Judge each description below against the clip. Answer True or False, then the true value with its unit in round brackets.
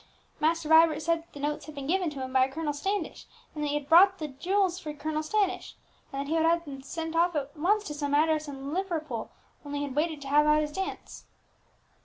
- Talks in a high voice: True (310 Hz)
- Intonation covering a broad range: False (2.6 semitones)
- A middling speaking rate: False (245 wpm)